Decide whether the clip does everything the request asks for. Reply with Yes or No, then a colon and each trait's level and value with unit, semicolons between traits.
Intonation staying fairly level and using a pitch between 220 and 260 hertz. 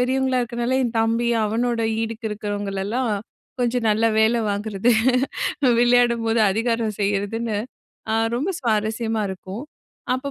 Yes: narrow, 2.2 semitones; high, 230 Hz